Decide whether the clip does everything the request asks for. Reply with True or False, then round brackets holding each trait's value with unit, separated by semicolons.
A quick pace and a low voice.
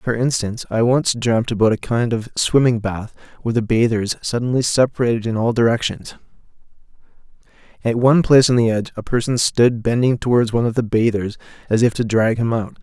False (185 wpm; 115 Hz)